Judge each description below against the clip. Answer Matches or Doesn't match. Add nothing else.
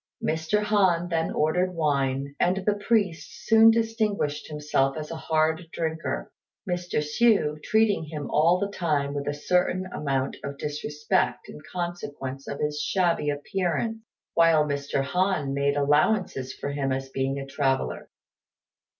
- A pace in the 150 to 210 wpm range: Doesn't match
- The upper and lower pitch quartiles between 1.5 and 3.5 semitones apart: Doesn't match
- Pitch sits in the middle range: Matches